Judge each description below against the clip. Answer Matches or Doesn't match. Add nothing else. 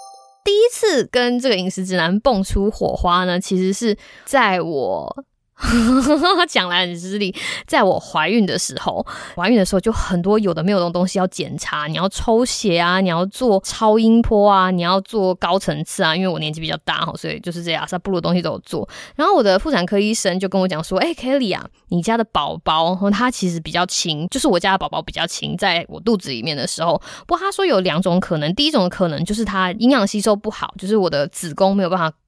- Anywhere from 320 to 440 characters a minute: Matches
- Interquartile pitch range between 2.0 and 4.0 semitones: Doesn't match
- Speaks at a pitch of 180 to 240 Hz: Matches